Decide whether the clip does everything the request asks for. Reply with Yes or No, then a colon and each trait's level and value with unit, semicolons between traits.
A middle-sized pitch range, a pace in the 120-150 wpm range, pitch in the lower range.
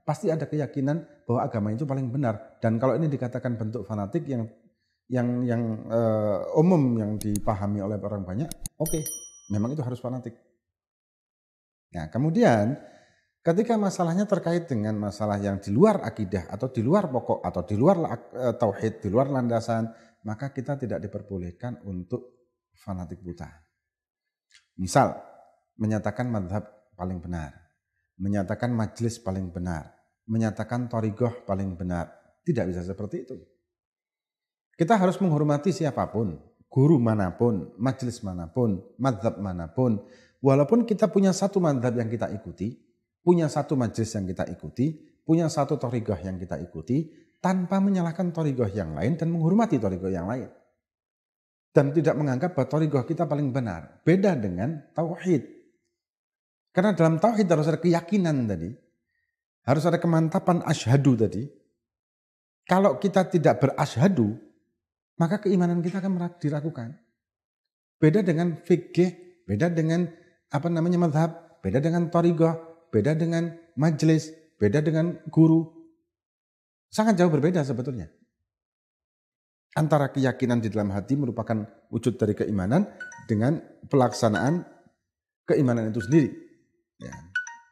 No: wide, 7.7 semitones; average, 125 wpm; low, 130 Hz